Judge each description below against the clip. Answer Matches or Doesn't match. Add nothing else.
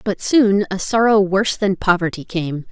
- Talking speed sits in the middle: Matches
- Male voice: Doesn't match